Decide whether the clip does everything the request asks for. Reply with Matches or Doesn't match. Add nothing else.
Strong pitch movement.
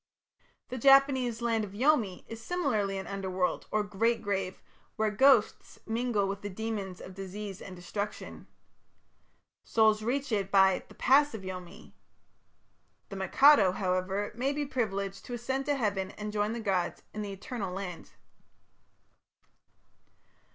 Doesn't match